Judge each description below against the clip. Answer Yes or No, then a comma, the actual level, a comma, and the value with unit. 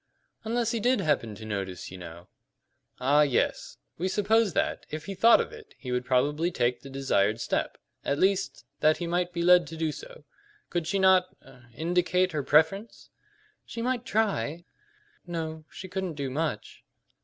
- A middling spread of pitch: No, wide, 6.1 semitones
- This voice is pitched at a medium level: Yes, medium, 165 Hz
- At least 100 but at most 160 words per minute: No, average, 175 wpm